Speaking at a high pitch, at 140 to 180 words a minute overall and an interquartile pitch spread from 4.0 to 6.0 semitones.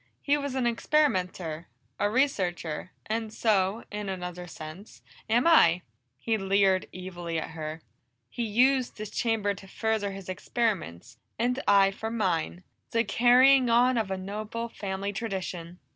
Yes: high, 200 Hz; average, 145 wpm; average, 4.3 semitones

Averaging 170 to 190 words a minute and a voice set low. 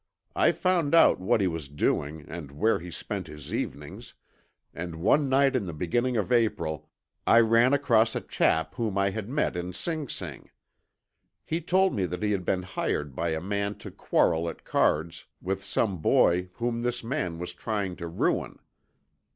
Yes: average, 180 wpm; low, 100 Hz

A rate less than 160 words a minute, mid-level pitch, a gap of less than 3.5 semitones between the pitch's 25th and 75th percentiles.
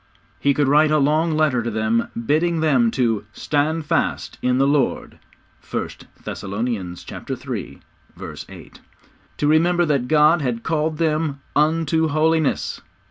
No: slow, 135 wpm; medium, 150 Hz; average, 4.0 semitones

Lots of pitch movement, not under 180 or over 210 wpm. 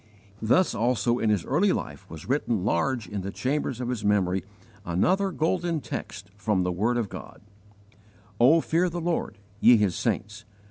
No: wide, 6.6 semitones; average, 170 wpm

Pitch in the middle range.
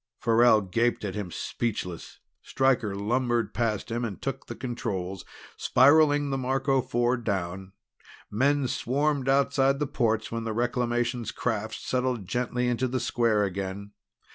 No: low, 120 Hz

